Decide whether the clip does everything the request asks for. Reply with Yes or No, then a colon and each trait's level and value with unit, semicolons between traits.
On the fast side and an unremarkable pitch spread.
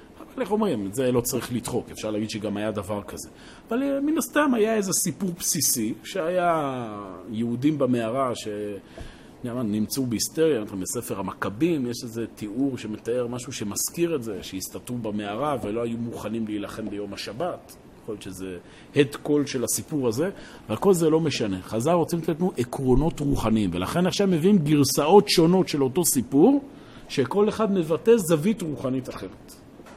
No: fast, 155 wpm; wide, 8.2 semitones